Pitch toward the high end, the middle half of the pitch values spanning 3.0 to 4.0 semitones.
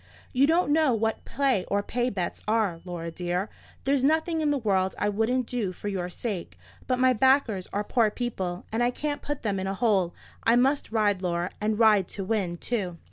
No: high, 215 Hz; average, 5.1 semitones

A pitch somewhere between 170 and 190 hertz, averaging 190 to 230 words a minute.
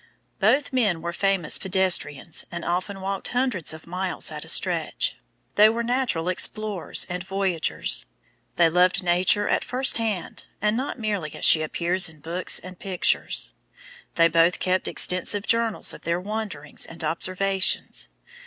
No: medium, 185 Hz; average, 150 wpm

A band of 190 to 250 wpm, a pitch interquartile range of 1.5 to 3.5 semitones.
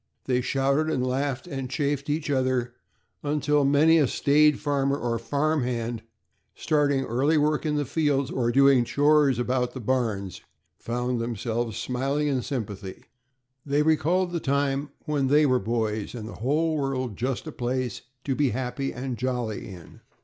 No: average, 160 wpm; average, 3.1 semitones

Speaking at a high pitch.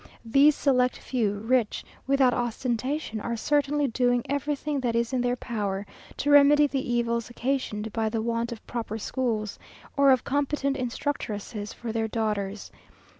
Yes: high, 245 Hz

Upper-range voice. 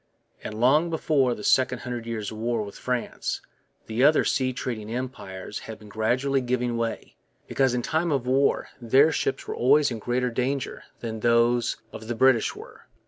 No: low, 125 Hz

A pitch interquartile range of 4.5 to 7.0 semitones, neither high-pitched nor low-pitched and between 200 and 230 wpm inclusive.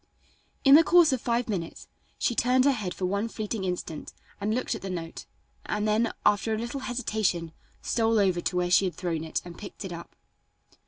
No: average, 4.8 semitones; high, 210 Hz; fast, 205 wpm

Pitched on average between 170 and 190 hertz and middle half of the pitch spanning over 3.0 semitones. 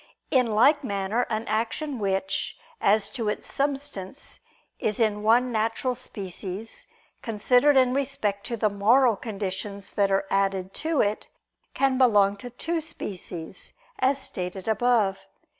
No: high, 220 Hz; average, 4.3 semitones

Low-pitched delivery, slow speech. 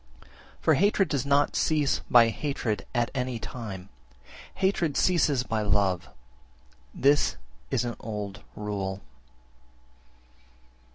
Yes: low, 120 Hz; slow, 110 wpm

